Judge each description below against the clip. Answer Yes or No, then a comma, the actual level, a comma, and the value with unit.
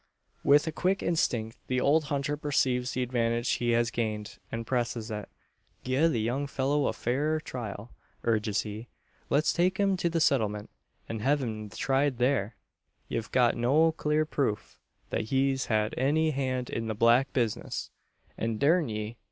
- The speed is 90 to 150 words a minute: No, average, 165 wpm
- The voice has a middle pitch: No, low, 125 Hz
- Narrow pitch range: No, average, 4.2 semitones